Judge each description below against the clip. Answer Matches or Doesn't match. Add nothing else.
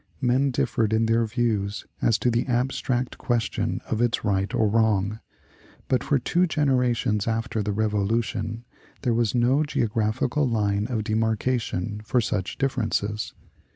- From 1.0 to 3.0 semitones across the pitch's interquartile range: Matches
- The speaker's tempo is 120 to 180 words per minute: Matches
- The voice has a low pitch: Matches